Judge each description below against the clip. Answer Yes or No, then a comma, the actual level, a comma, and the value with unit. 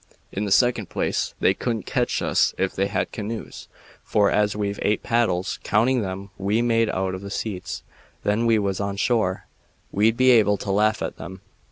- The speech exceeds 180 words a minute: Yes, average, 190 wpm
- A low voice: Yes, low, 105 Hz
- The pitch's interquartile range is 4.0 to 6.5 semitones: No, average, 2.7 semitones